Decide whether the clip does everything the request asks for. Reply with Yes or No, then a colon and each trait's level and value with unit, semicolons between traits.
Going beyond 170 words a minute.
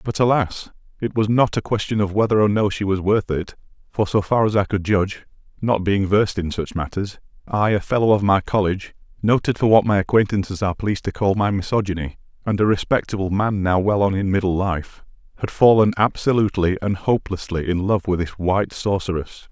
Yes: fast, 205 wpm